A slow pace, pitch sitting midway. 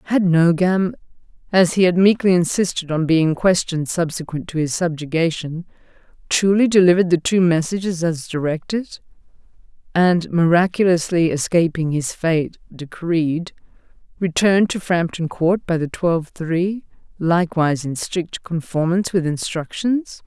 Yes: slow, 120 wpm; medium, 170 Hz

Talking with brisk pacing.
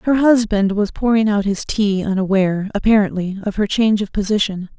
No: average, 175 wpm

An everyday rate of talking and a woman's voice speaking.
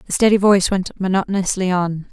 Yes: average, 170 wpm; female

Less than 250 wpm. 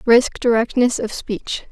Yes: average, 140 wpm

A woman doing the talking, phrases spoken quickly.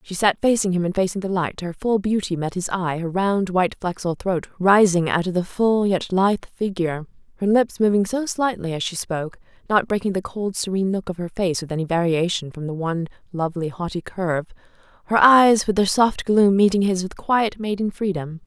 Yes: female; fast, 210 wpm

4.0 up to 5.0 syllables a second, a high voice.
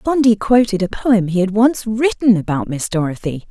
Yes: 4.9 syllables/s; high, 210 Hz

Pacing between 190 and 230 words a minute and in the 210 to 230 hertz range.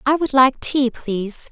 No: average, 200 wpm; very high, 255 Hz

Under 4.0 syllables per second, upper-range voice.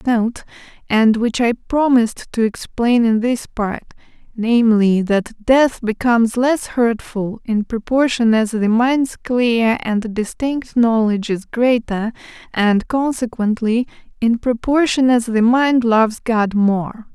Yes: 3.8 syllables/s; high, 230 Hz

